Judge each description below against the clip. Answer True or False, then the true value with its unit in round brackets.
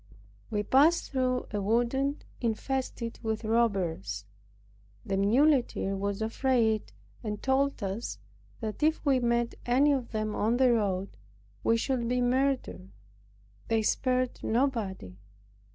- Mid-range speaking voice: False (235 Hz)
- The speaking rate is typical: False (120 wpm)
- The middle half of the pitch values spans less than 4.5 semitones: True (3.8 semitones)